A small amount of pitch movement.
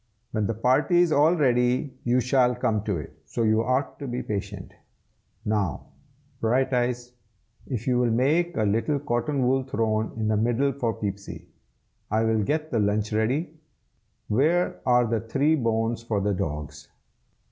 No: average, 3.6 semitones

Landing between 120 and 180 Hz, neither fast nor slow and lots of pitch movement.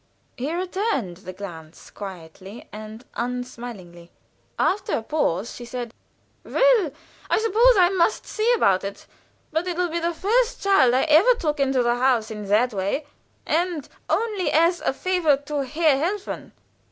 No: very high, 280 Hz; average, 155 wpm; wide, 8.7 semitones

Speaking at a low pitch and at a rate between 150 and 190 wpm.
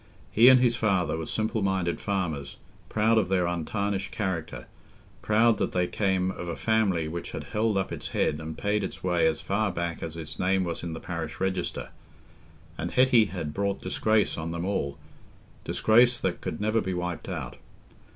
Yes: very low, 95 Hz; average, 180 wpm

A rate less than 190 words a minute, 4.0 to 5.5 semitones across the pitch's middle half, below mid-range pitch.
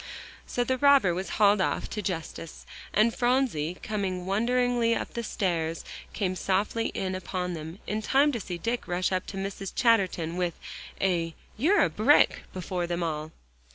No: average, 165 wpm; average, 4.6 semitones; high, 190 Hz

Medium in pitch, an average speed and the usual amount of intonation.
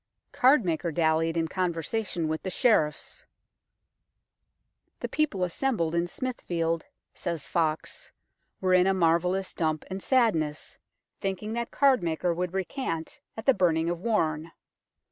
No: medium, 175 Hz; slow, 125 wpm; average, 4.4 semitones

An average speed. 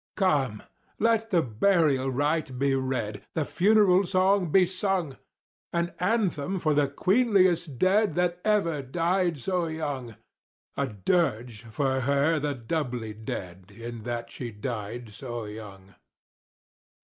No: slow, 125 wpm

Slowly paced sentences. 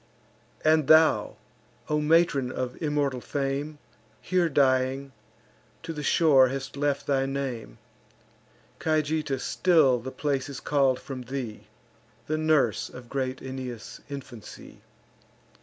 Yes: slow, 115 wpm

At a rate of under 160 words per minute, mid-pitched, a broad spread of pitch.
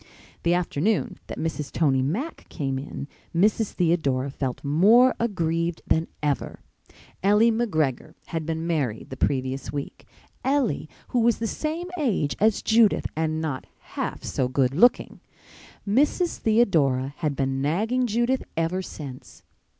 Yes: slow, 135 wpm; medium, 165 Hz; wide, 8.0 semitones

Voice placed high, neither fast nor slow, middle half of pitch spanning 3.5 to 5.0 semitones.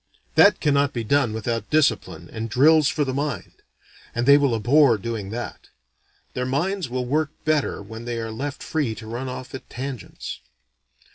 No: low, 125 Hz; average, 170 wpm; average, 3.9 semitones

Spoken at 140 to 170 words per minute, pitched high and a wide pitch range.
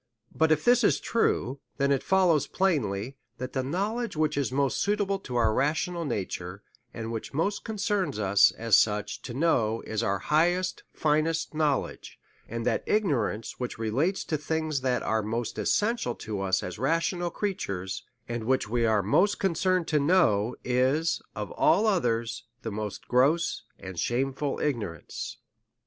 No: average, 160 wpm; low, 135 Hz; wide, 7.1 semitones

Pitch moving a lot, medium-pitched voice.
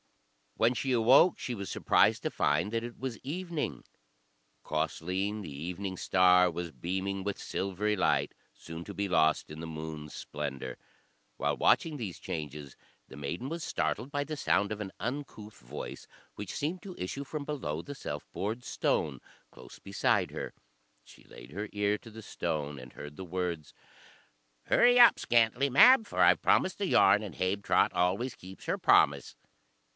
No: wide, 7.1 semitones; low, 100 Hz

